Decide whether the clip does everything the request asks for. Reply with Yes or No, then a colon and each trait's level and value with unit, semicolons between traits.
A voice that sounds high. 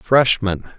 No: low, 115 Hz